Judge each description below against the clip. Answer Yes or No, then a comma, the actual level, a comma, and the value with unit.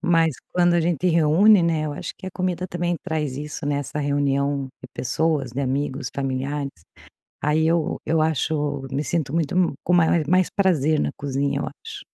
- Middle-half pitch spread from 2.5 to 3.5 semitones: Yes, average, 3.1 semitones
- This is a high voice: No, medium, 155 Hz